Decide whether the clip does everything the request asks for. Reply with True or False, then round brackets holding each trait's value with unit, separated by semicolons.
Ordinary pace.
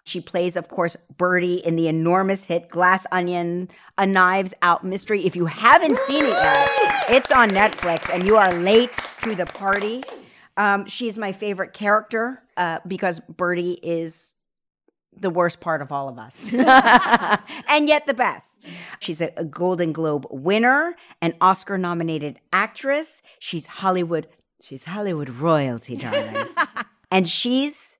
True (145 wpm)